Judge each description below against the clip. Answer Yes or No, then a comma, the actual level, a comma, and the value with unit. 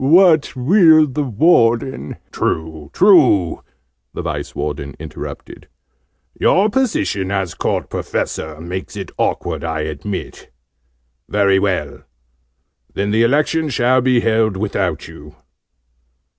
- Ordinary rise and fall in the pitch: No, wide, 8.8 semitones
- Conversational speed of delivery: No, slow, 115 wpm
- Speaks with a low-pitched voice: Yes, low, 105 Hz